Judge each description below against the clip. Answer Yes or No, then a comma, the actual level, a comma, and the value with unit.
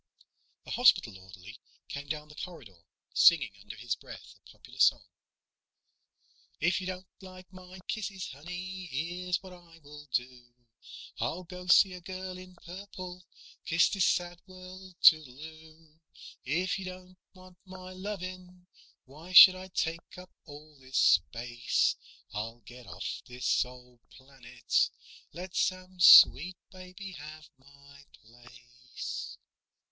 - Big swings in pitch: Yes, wide, 5.9 semitones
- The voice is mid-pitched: Yes, medium, 170 Hz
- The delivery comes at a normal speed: No, slow, 130 wpm